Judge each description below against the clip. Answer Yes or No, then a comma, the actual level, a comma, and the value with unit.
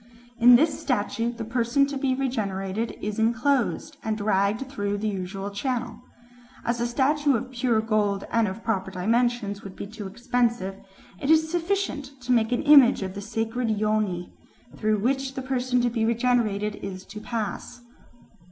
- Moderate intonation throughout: Yes, average, 3.6 semitones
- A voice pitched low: No, high, 230 Hz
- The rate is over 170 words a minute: No, average, 165 wpm